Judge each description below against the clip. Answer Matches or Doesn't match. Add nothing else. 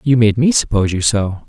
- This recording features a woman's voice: Doesn't match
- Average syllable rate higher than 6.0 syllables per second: Doesn't match